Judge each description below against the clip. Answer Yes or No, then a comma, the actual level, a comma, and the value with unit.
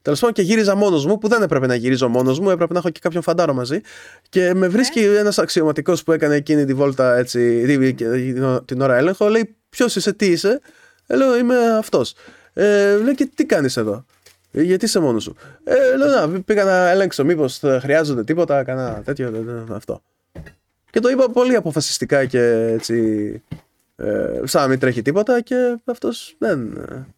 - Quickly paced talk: Yes, fast, 185 wpm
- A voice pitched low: No, medium, 170 Hz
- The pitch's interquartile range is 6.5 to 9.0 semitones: Yes, wide, 8.3 semitones